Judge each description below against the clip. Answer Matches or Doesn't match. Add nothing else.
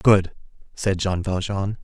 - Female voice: Doesn't match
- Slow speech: Matches